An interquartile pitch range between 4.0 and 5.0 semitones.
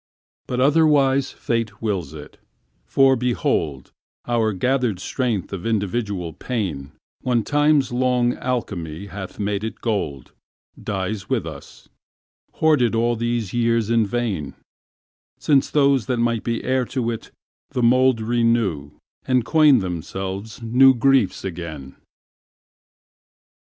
Yes: average, 4.6 semitones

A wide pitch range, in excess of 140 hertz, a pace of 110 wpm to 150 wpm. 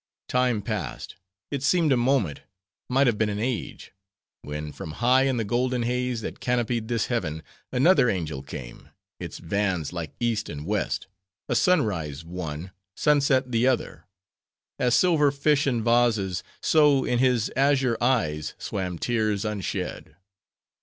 No: wide, 5.8 semitones; low, 115 Hz; average, 145 wpm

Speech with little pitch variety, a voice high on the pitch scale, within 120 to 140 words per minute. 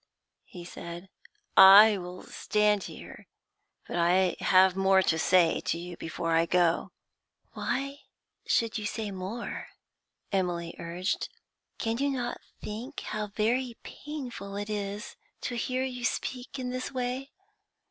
No: average, 5.2 semitones; high, 205 Hz; slow, 135 wpm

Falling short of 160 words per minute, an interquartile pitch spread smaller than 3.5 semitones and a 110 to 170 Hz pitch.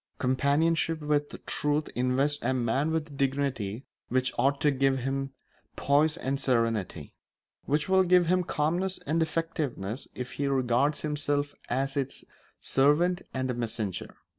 Yes: average, 140 wpm; average, 2.9 semitones; medium, 140 Hz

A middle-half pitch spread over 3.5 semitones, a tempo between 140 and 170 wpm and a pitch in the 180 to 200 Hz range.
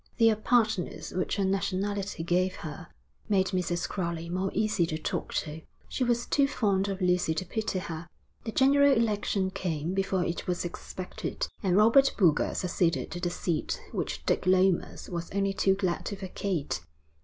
No: average, 2.9 semitones; average, 165 wpm; high, 190 Hz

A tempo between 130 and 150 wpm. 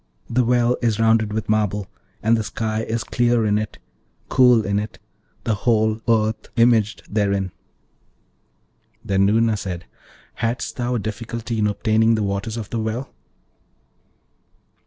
Yes: average, 140 wpm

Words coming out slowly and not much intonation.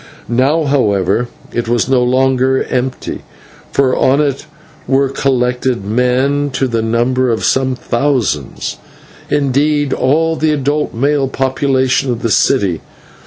Yes: slow, 125 wpm; narrow, 2.2 semitones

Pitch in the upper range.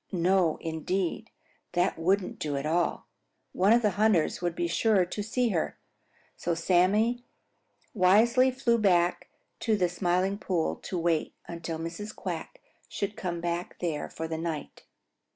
No: medium, 180 Hz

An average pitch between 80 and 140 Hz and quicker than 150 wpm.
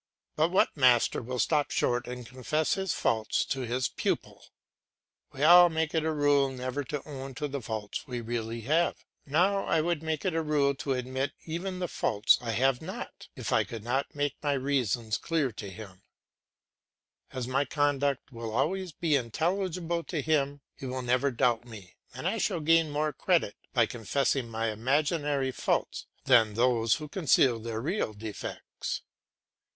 Yes: low, 135 Hz; average, 170 wpm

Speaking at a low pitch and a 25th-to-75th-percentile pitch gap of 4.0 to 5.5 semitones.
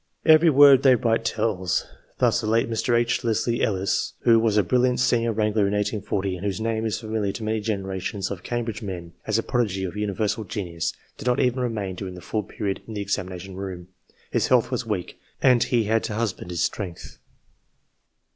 No: low, 110 Hz; average, 3.3 semitones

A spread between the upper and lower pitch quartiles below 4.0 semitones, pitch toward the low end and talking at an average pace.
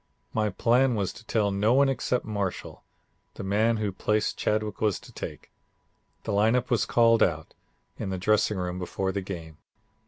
Yes: average, 3.0 semitones; low, 105 Hz; average, 175 wpm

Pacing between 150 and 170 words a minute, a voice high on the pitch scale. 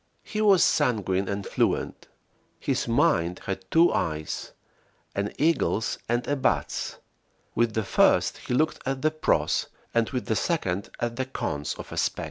No: average, 160 wpm; low, 120 Hz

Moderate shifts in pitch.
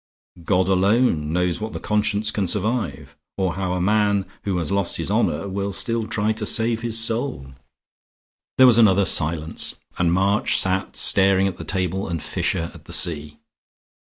Yes: average, 3.6 semitones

